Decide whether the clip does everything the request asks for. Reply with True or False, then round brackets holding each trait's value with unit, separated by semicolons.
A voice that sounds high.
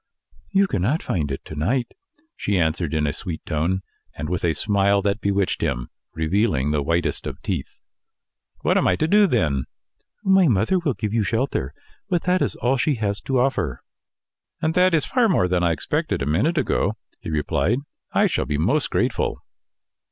False (100 Hz)